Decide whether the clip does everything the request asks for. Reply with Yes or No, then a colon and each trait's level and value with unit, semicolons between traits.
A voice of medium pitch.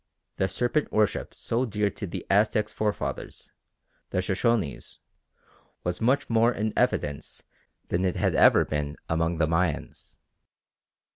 No: low, 100 Hz